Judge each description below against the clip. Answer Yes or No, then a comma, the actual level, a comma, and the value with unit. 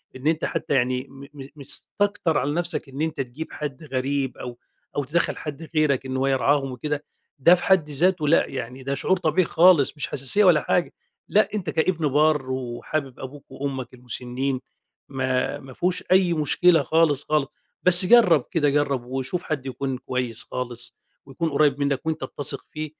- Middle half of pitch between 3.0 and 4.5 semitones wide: Yes, average, 3.4 semitones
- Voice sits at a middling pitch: Yes, medium, 145 Hz